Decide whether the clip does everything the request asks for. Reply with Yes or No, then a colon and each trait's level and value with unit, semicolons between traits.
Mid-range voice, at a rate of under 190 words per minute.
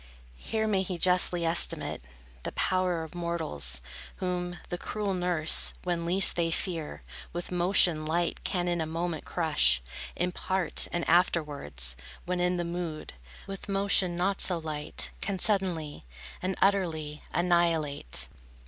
Yes: medium, 175 Hz; average, 140 wpm